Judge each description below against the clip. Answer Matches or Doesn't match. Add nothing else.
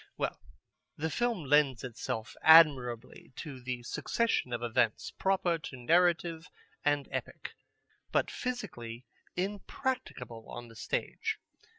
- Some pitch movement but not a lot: Doesn't match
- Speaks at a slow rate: Matches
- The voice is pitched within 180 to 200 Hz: Doesn't match